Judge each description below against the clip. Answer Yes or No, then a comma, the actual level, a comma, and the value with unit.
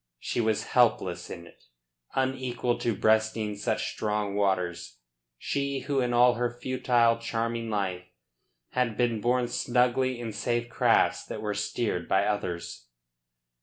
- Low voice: Yes, low, 115 Hz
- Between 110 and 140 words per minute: Yes, slow, 135 wpm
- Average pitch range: Yes, average, 3.0 semitones